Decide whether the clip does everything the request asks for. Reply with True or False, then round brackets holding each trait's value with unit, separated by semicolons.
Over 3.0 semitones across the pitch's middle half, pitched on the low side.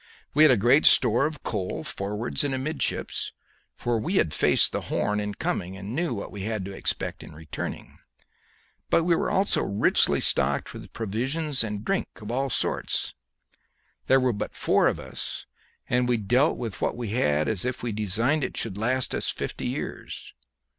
True (4.6 semitones; 115 Hz)